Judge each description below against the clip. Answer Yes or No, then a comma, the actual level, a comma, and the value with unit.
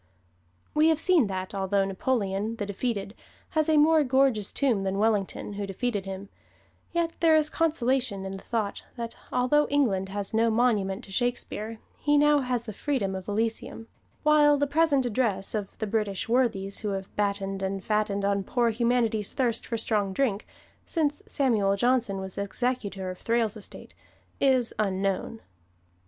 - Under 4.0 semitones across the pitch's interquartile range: No, average, 4.7 semitones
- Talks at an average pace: Yes, average, 160 wpm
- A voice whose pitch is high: Yes, high, 225 Hz